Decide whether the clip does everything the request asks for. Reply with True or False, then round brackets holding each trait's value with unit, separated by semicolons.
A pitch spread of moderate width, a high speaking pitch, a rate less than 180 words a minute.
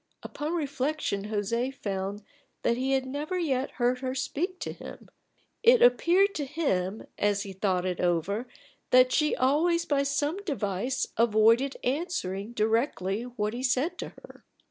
False (5.9 semitones; 255 Hz; 150 wpm)